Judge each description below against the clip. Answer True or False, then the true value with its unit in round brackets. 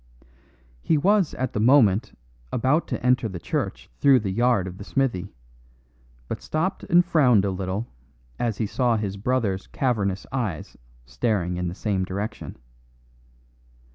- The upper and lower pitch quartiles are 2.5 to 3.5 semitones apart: False (5.3 semitones)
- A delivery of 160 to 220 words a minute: False (145 wpm)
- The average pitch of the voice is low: True (110 Hz)